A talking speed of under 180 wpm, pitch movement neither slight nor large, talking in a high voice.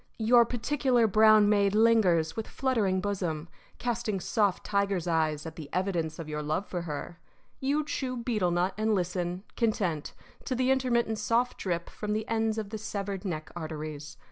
Yes: average, 170 wpm; average, 4.8 semitones; high, 200 Hz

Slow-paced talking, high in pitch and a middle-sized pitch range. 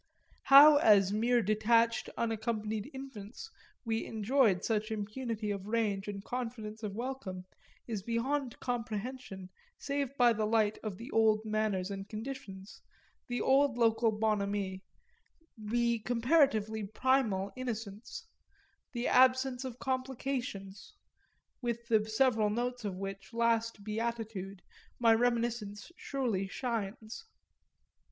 Yes: slow, 115 wpm; high, 225 Hz; average, 3.0 semitones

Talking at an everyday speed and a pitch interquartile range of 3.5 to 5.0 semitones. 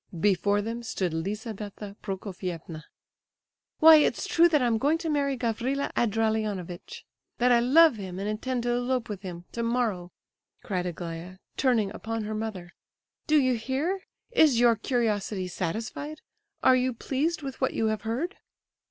Yes: average, 150 wpm; average, 4.7 semitones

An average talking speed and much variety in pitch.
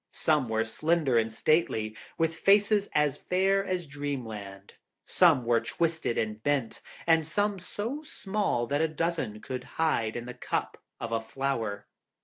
Yes: average, 150 wpm; wide, 7.0 semitones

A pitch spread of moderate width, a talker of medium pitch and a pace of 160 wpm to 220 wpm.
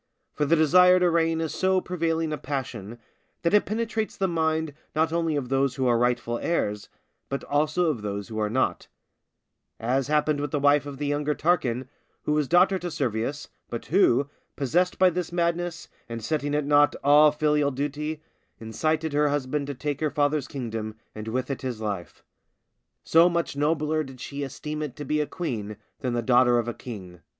Yes: average, 4.1 semitones; medium, 145 Hz; average, 190 wpm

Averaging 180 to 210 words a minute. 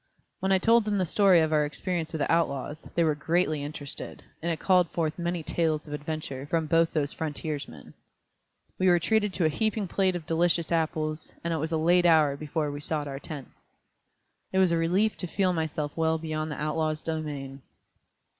Yes: average, 200 wpm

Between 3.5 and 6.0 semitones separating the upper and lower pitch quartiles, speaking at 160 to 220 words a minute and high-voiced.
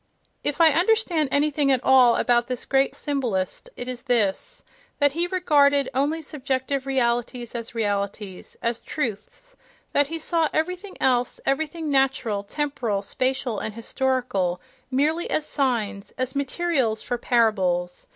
No: average, 4.2 semitones; slow, 135 wpm; very high, 265 Hz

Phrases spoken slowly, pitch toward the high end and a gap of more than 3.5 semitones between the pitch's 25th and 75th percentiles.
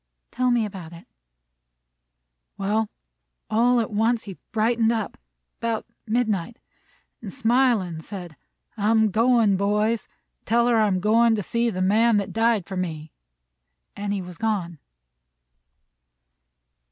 No: slow, 125 wpm; high, 215 Hz; average, 3.2 semitones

